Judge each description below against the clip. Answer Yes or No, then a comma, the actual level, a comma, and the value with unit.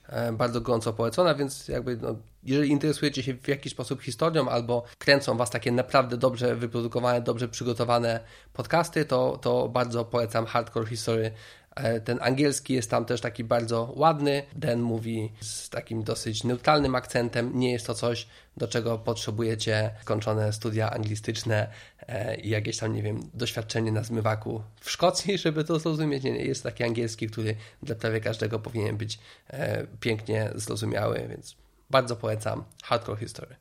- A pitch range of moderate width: No, narrow, 2.3 semitones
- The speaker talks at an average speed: Yes, average, 150 wpm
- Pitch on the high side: No, low, 120 Hz